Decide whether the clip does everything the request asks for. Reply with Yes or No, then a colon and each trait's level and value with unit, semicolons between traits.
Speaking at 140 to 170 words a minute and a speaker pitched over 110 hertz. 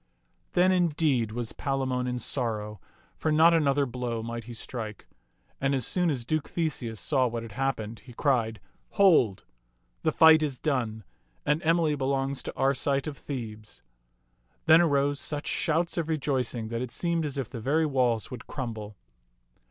Yes: average, 165 wpm; low, 135 Hz